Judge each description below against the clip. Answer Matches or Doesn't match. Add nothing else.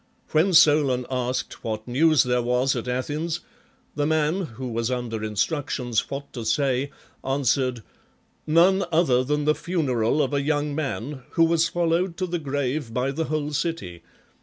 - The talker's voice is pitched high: Doesn't match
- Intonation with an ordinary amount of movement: Matches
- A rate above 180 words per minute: Doesn't match